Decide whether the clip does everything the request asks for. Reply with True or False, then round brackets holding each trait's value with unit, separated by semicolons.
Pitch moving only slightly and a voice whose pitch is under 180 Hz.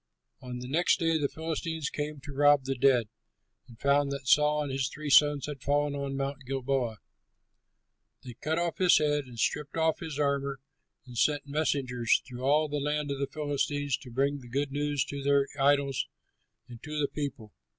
True (1.7 semitones; 140 Hz)